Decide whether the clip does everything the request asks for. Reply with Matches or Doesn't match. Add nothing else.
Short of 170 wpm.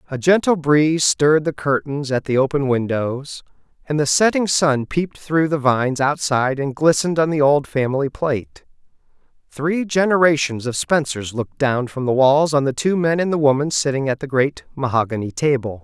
Doesn't match